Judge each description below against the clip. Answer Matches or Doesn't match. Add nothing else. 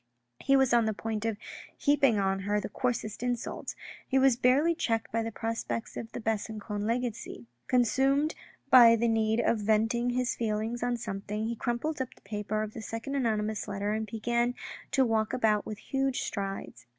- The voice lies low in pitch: Doesn't match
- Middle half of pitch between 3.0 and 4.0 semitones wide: Doesn't match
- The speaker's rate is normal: Matches